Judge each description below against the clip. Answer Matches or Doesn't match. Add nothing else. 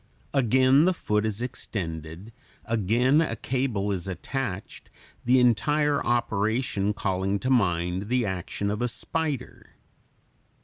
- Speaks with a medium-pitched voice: Doesn't match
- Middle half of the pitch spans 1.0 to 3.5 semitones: Doesn't match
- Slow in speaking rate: Matches